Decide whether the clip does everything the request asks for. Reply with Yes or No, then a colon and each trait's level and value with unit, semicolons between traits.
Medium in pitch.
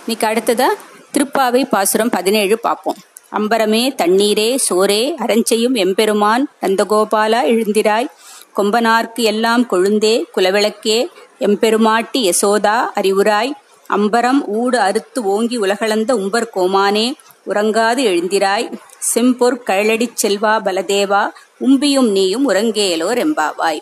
No: high, 220 Hz